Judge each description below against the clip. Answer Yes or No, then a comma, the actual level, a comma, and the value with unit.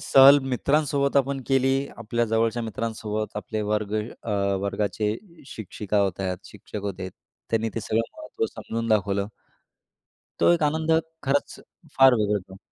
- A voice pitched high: No, low, 110 Hz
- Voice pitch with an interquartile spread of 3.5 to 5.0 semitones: Yes, average, 4.3 semitones